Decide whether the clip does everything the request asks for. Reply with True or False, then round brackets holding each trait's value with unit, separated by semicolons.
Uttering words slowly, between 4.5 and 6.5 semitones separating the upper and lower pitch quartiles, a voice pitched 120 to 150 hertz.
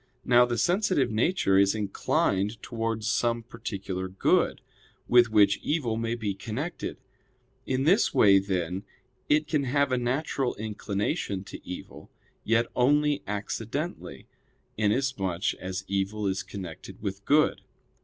False (125 wpm; 4.9 semitones; 110 Hz)